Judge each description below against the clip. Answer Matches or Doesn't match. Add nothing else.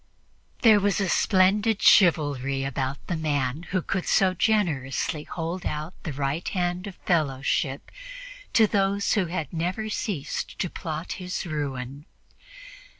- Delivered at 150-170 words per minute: Doesn't match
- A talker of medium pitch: Matches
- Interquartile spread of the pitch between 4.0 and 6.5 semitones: Matches